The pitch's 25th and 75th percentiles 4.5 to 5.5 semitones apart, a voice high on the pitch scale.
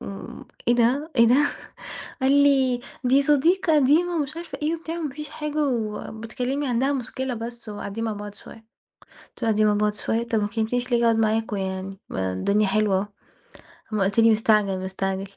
Yes: average, 4.8 semitones; high, 230 Hz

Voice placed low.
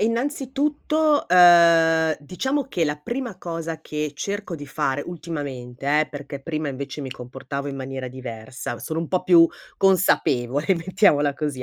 No: medium, 155 Hz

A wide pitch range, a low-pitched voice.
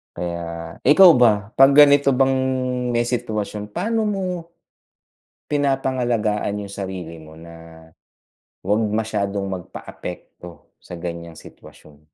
Yes: wide, 7.6 semitones; low, 105 Hz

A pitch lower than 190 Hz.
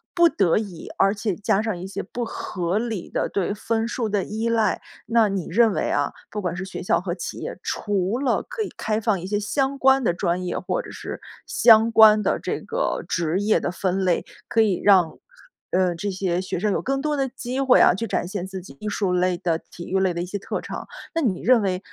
No: high, 200 Hz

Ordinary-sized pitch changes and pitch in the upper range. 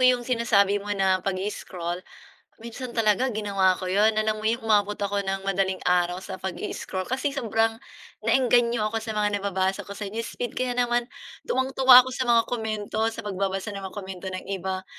Yes: average, 3.4 semitones; high, 210 Hz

